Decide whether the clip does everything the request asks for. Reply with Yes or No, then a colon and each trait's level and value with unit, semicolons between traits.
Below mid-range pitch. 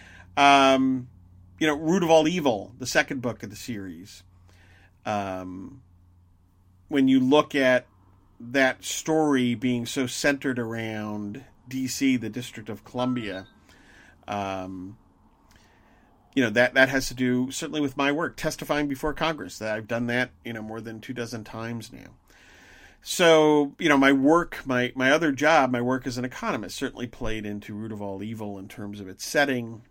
Yes: low, 125 Hz